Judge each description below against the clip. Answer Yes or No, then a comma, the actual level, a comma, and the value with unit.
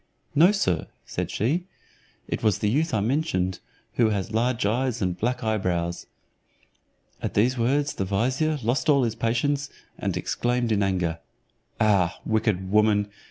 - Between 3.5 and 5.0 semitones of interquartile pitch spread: Yes, average, 4.5 semitones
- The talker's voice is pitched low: Yes, low, 110 Hz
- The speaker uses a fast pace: No, average, 145 wpm